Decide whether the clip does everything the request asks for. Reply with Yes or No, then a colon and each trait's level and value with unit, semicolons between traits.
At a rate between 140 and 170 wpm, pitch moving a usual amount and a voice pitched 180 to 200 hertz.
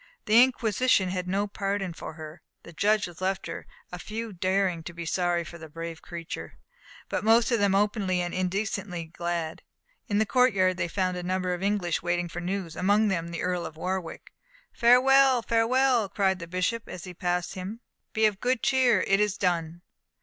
No: average, 185 wpm; average, 3.5 semitones; medium, 185 Hz